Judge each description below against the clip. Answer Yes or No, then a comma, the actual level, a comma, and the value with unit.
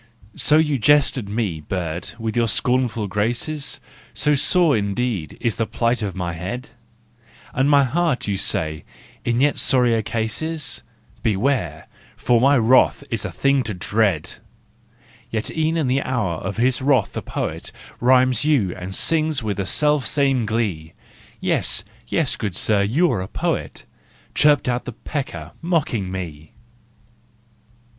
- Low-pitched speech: Yes, low, 120 Hz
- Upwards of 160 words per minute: No, average, 150 wpm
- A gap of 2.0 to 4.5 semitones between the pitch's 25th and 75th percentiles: No, wide, 5.5 semitones